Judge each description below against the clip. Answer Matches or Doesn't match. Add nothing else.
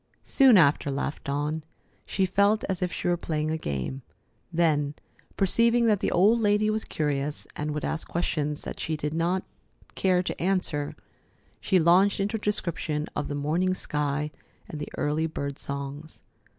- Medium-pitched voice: Matches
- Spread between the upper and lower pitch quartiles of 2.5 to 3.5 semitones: Doesn't match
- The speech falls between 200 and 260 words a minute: Doesn't match